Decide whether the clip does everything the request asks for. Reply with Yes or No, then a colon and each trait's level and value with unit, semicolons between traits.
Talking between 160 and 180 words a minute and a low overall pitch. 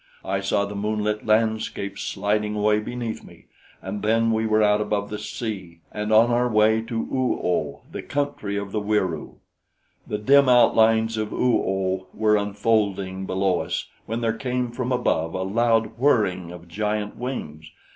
Yes: average, 165 wpm; low, 105 Hz